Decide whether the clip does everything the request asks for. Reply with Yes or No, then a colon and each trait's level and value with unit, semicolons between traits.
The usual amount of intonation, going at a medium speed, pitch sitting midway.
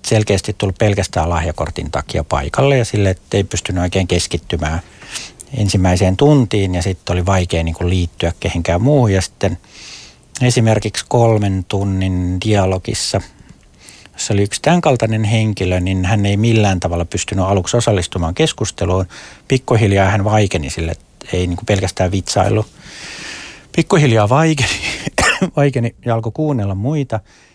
No: average, 3.9 semitones; average, 125 wpm; low, 100 Hz